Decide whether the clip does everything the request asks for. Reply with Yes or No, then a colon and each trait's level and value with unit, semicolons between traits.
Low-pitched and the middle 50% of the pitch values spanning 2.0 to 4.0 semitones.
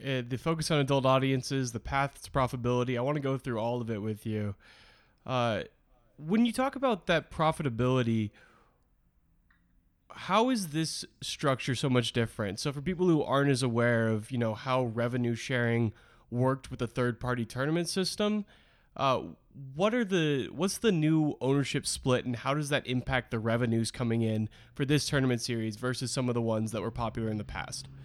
Yes: low, 130 Hz; average, 3.7 semitones